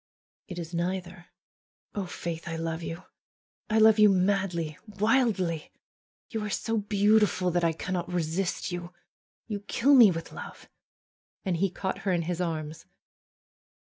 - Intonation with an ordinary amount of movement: Yes, average, 3.3 semitones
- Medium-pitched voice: Yes, medium, 180 Hz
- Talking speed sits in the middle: Yes, average, 145 wpm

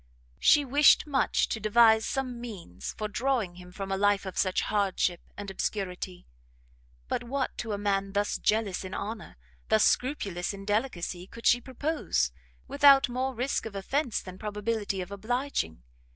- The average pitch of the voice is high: Yes, high, 210 Hz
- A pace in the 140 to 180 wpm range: Yes, average, 160 wpm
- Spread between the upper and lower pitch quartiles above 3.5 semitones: Yes, average, 4.3 semitones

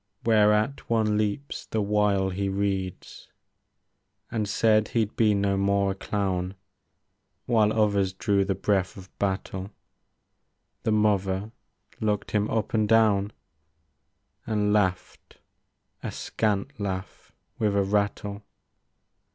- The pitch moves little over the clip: Yes, narrow, 1.6 semitones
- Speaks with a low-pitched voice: Yes, low, 105 Hz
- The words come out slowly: Yes, slow, 120 wpm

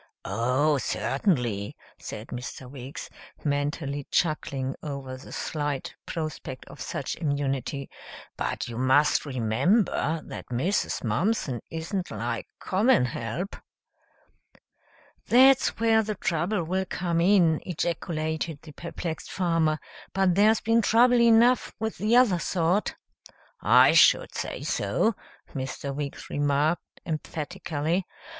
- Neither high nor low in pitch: Yes, medium, 160 Hz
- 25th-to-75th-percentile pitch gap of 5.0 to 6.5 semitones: Yes, wide, 5.6 semitones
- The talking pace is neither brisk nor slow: No, slow, 115 wpm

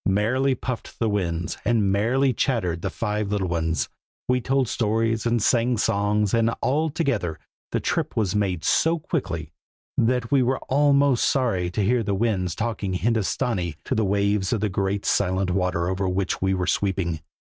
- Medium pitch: No, low, 105 Hz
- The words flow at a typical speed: Yes, average, 170 wpm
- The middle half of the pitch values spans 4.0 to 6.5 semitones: Yes, average, 4.5 semitones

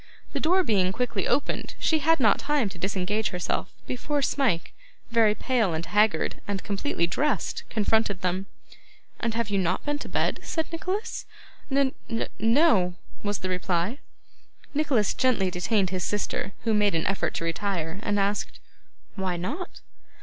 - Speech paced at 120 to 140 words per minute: No, average, 155 wpm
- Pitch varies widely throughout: Yes, wide, 5.8 semitones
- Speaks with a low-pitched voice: No, high, 210 Hz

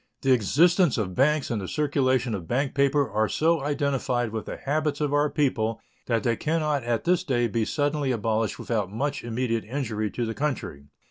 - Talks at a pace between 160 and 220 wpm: Yes, average, 195 wpm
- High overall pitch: No, low, 130 Hz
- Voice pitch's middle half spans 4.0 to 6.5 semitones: Yes, average, 4.5 semitones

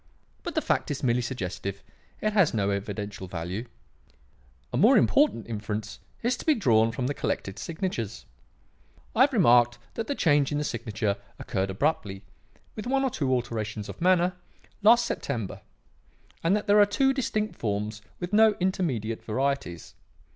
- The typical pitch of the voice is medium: No, low, 125 Hz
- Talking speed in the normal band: Yes, average, 160 wpm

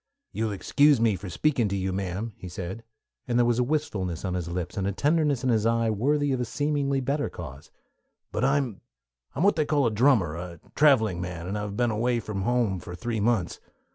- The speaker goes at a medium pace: No, fast, 225 wpm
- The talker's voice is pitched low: Yes, low, 115 Hz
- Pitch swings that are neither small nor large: No, wide, 6.1 semitones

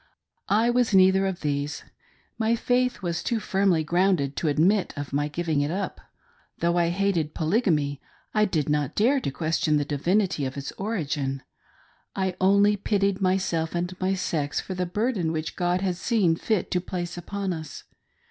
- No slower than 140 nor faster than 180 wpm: Yes, average, 170 wpm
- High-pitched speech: No, medium, 180 Hz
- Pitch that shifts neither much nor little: Yes, average, 4.2 semitones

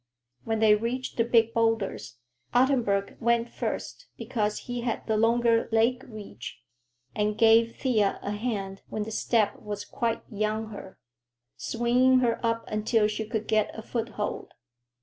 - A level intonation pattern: Yes, narrow, 1.9 semitones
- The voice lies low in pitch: No, high, 225 Hz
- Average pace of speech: Yes, average, 150 wpm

